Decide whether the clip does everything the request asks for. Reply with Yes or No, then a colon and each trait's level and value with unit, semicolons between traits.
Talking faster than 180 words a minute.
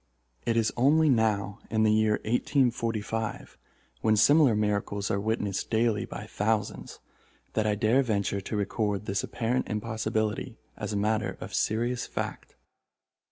No: average, 140 wpm